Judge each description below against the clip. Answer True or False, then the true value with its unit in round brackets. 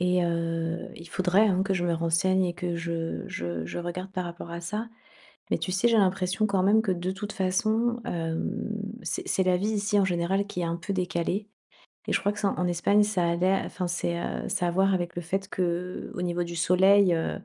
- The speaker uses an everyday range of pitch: False (2.2 semitones)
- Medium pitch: True (180 Hz)